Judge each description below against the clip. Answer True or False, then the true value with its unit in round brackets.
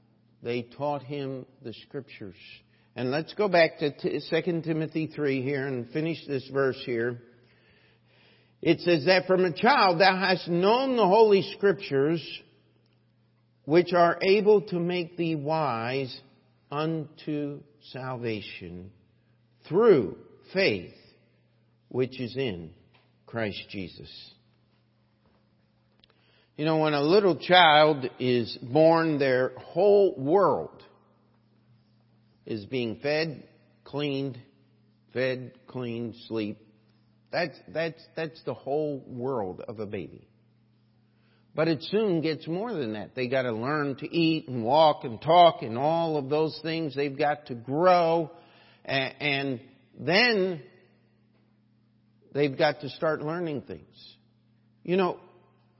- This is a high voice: False (135 Hz)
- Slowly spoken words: True (120 wpm)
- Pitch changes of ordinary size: False (5.9 semitones)